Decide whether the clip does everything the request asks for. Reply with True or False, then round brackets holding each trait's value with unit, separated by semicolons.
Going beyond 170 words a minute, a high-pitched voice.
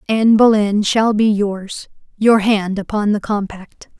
False (150 wpm; 210 Hz)